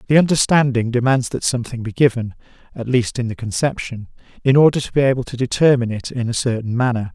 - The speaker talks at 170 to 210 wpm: Yes, average, 200 wpm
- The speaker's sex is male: Yes, male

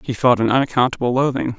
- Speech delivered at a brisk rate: No, average, 190 wpm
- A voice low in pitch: Yes, low, 125 Hz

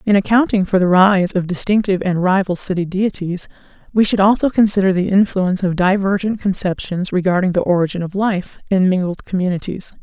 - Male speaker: No, female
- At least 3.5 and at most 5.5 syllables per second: No, 5.7 syllables/s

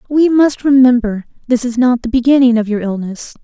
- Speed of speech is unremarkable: Yes, average, 190 wpm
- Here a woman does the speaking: Yes, female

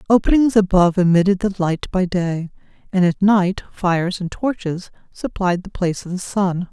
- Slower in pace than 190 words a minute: Yes, average, 170 wpm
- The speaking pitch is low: No, medium, 185 Hz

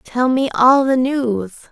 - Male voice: No, female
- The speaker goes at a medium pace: Yes, average, 175 wpm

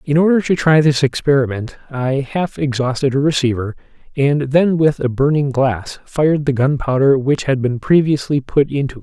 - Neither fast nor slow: Yes, average, 180 wpm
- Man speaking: Yes, male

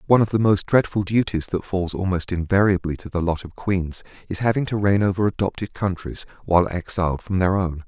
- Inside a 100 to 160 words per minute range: No, fast, 205 wpm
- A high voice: No, very low, 95 Hz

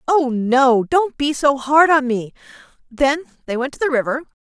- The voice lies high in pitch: Yes, very high, 270 Hz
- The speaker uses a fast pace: No, average, 190 wpm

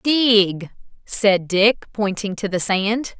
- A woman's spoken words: Yes, female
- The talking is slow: Yes, slow, 130 wpm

